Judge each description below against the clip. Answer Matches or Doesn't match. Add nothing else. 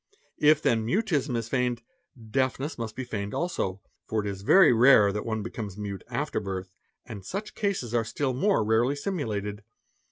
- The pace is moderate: Matches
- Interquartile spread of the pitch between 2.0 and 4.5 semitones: Doesn't match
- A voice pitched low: Matches